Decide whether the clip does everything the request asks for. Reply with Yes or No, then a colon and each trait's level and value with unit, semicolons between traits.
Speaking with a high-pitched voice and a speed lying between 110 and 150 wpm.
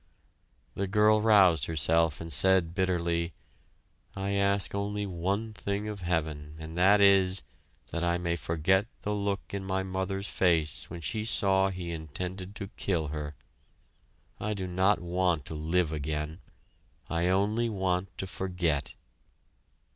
No: very low, 95 Hz; average, 140 wpm